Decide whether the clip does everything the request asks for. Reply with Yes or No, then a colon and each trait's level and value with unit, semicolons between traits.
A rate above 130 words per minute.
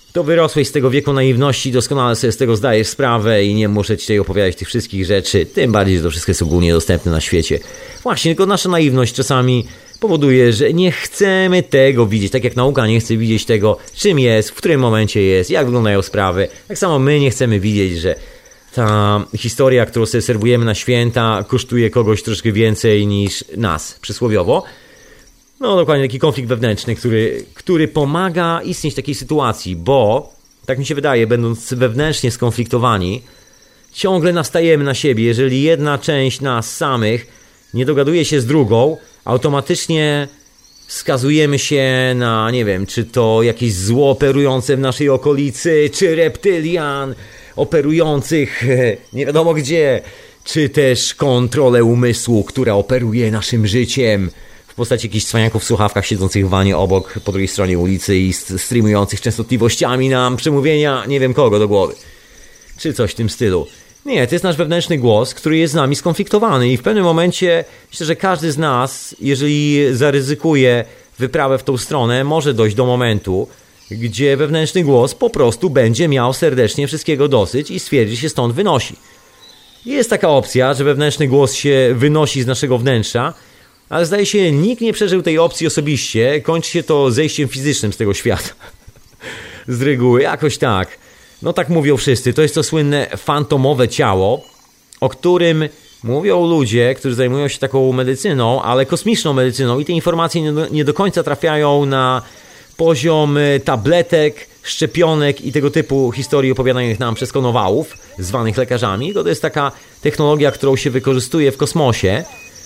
Yes: fast, 160 wpm